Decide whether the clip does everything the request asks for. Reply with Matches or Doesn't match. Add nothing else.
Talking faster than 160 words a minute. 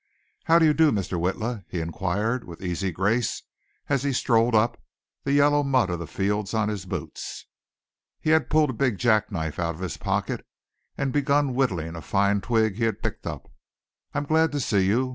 Matches